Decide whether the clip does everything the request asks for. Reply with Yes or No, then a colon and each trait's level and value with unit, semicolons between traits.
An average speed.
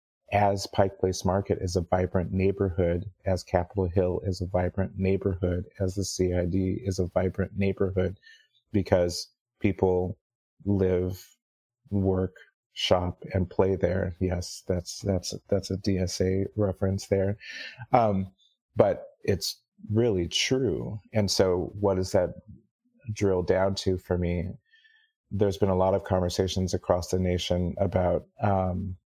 No: slow, 130 wpm